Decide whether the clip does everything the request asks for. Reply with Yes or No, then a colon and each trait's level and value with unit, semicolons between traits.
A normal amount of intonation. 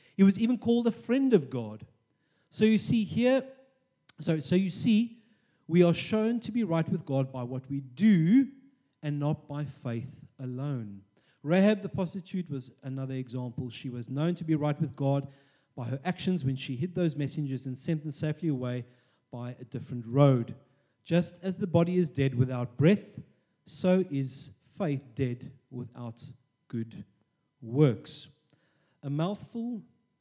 No: wide, 6.0 semitones